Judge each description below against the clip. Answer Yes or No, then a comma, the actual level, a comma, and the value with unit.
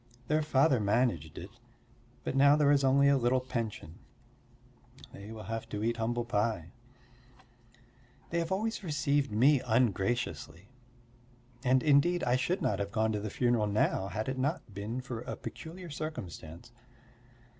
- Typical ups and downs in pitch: Yes, average, 5.0 semitones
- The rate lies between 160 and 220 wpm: No, average, 150 wpm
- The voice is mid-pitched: No, low, 120 Hz